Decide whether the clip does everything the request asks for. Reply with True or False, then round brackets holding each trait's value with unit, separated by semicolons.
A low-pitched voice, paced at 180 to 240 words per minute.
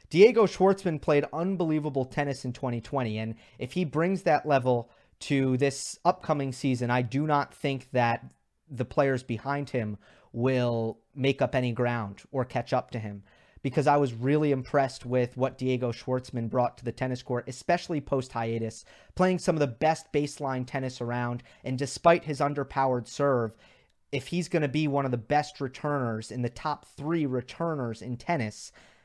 False (130 Hz; 170 wpm)